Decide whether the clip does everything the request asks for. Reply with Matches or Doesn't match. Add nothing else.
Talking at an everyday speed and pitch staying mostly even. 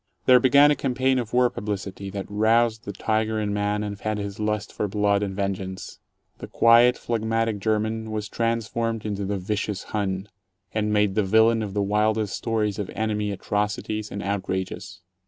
Matches